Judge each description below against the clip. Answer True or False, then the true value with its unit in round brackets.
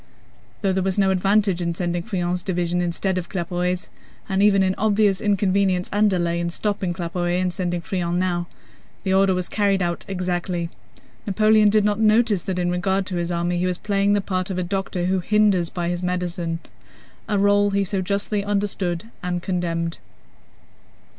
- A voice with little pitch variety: True (2.2 semitones)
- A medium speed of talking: True (175 wpm)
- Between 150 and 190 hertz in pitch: True (185 Hz)